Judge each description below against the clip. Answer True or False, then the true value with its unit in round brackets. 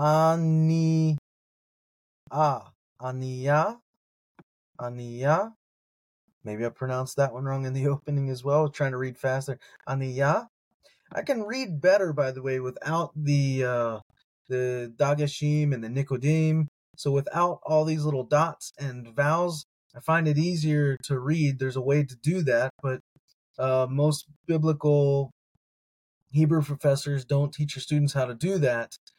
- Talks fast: False (140 wpm)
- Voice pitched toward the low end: False (145 Hz)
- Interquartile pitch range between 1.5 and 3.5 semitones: True (3.1 semitones)